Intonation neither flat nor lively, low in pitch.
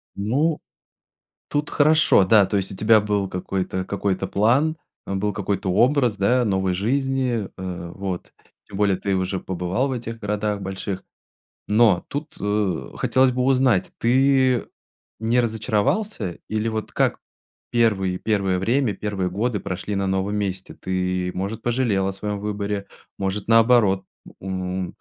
Yes: average, 3.7 semitones; low, 105 Hz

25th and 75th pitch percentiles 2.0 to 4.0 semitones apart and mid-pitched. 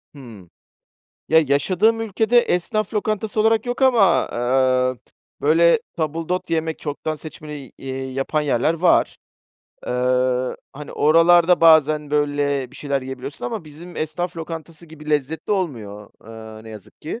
No: average, 4.6 semitones; medium, 155 Hz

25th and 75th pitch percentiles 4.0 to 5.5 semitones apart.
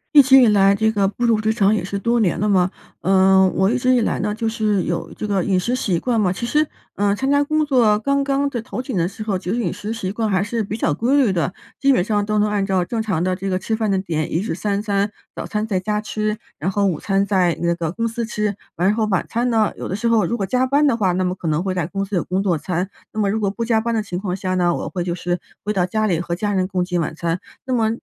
No: average, 3.4 semitones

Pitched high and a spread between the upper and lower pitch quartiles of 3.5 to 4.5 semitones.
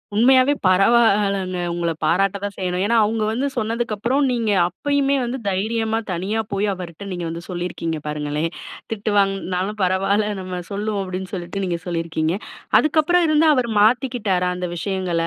Yes: high, 200 Hz; average, 4.1 semitones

